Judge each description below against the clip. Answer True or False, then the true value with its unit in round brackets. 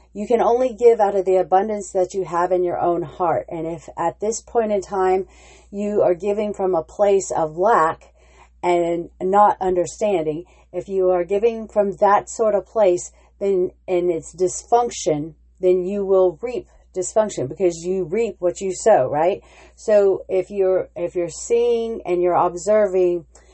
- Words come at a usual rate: True (170 wpm)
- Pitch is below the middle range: False (185 Hz)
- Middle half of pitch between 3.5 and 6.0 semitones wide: False (2.7 semitones)